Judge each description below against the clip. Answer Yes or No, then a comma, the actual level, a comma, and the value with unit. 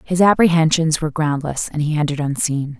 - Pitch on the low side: No, medium, 155 Hz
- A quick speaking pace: No, average, 170 wpm